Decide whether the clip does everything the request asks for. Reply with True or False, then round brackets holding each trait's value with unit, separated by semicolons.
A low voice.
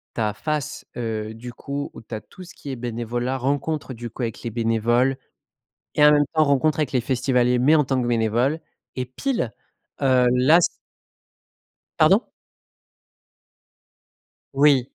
True (130 Hz)